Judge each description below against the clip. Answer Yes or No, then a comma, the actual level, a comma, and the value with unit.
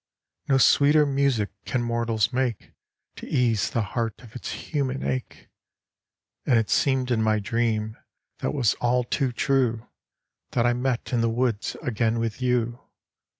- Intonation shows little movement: Yes, narrow, 2.3 semitones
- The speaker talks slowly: No, average, 150 wpm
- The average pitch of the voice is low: Yes, low, 120 Hz